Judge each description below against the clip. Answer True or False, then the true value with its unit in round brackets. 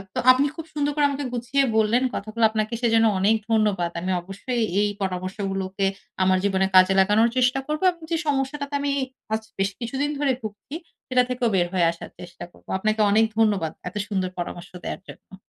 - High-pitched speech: True (215 Hz)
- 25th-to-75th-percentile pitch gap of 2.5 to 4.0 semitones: False (5.0 semitones)